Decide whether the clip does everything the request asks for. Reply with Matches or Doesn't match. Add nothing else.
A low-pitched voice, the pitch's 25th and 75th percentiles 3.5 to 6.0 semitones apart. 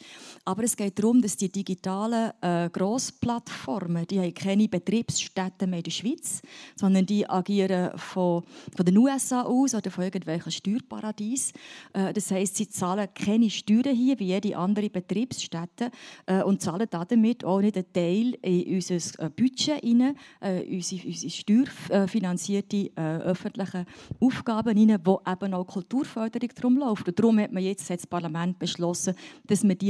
Doesn't match